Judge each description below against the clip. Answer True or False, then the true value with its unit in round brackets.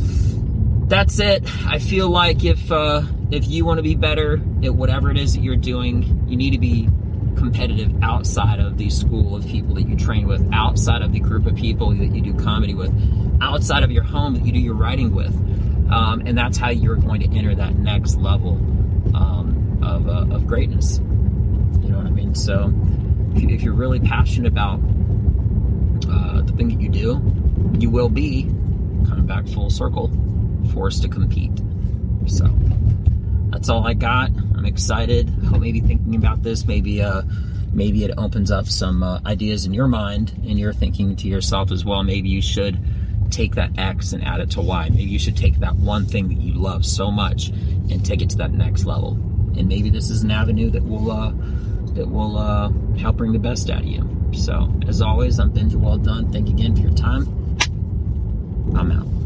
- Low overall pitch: True (100 Hz)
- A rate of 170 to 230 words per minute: True (195 wpm)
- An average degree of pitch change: False (1.9 semitones)